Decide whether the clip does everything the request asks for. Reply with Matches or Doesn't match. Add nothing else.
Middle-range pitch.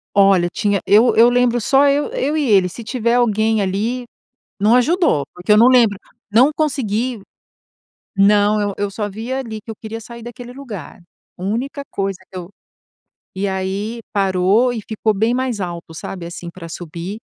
Doesn't match